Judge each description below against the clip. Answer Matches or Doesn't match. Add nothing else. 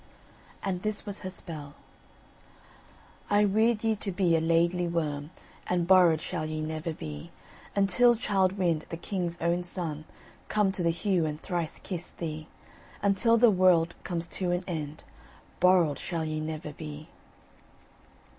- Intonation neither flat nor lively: Matches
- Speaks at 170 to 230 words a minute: Doesn't match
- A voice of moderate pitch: Matches